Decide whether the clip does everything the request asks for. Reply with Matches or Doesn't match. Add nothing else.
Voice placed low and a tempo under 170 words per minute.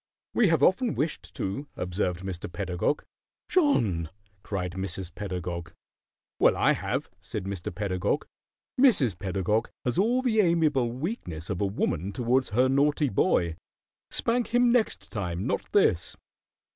Matches